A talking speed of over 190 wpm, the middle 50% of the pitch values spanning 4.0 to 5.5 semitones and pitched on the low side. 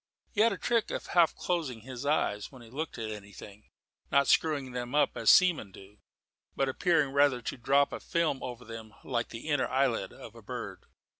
Yes: average, 200 wpm; average, 4.7 semitones; low, 130 Hz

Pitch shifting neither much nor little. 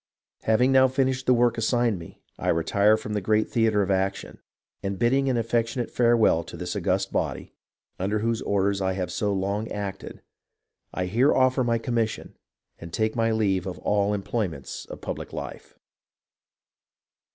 Yes: average, 3.3 semitones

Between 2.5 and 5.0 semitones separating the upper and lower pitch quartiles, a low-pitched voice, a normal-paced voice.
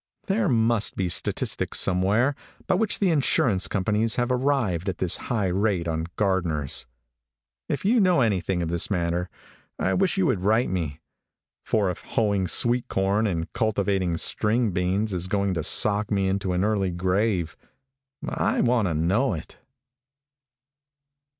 Yes: average, 4.2 semitones; low, 100 Hz; average, 150 wpm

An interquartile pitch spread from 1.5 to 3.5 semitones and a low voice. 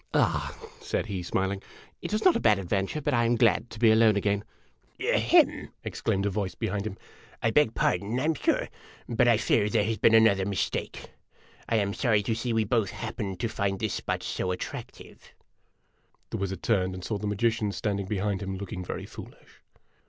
Yes: average, 2.7 semitones; low, 105 Hz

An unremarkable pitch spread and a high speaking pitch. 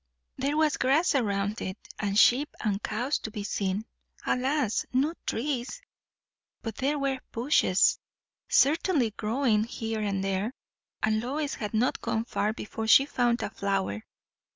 Yes: average, 4.6 semitones; high, 230 Hz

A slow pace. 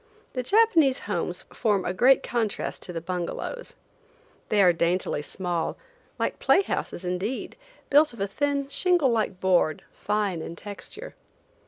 No: average, 145 wpm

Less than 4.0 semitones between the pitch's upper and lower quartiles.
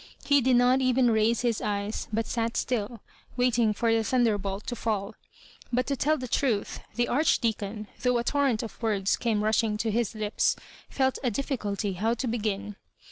Yes: average, 2.9 semitones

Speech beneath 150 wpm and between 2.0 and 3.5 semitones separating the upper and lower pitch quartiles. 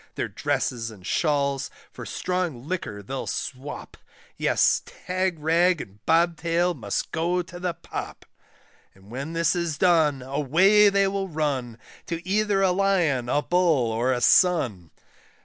No: average, 140 wpm; wide, 5.6 semitones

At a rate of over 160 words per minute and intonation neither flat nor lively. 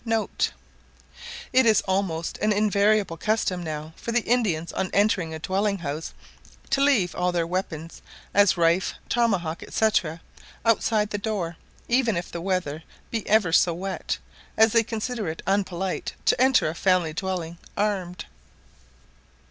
No: average, 145 wpm; average, 4.3 semitones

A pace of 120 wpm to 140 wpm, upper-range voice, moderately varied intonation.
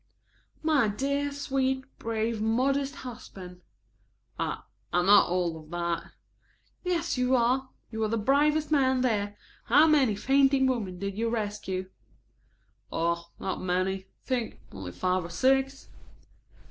No: slow, 135 wpm; high, 230 Hz; wide, 6.3 semitones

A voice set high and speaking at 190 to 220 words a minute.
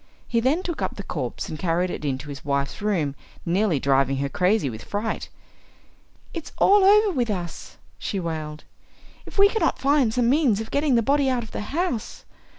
Yes: high, 215 Hz; average, 195 wpm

